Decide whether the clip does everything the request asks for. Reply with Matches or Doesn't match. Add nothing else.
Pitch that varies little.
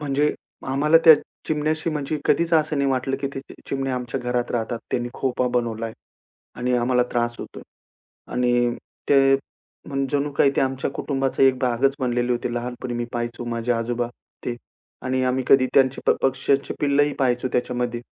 Matches